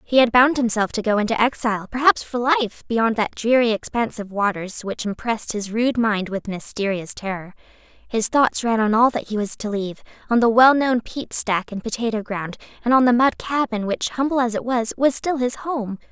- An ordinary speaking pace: No, fast, 215 wpm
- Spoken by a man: No, female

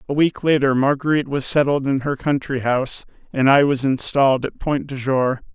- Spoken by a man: Yes, male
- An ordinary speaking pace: Yes, average, 195 wpm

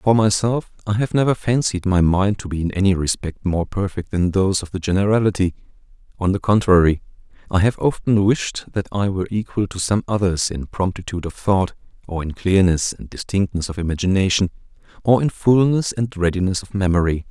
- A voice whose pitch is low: Yes, very low, 95 Hz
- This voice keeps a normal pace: Yes, average, 180 wpm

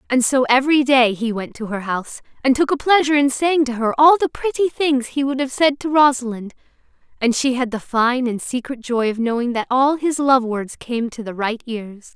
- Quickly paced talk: Yes, fast, 230 wpm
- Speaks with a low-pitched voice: No, very high, 255 Hz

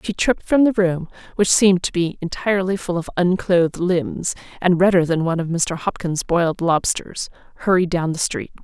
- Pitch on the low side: No, medium, 175 Hz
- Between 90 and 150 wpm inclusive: No, average, 190 wpm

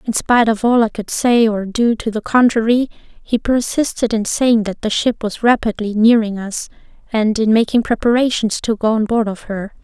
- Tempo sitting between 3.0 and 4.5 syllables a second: No, 5.0 syllables/s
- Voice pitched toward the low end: No, high, 225 Hz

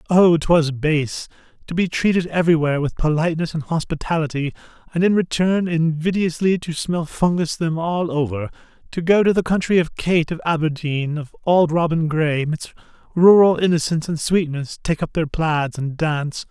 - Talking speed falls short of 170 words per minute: Yes, average, 160 wpm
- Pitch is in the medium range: Yes, medium, 160 Hz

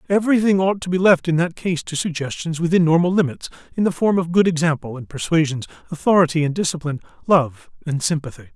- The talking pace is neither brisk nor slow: Yes, average, 190 wpm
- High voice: No, medium, 165 Hz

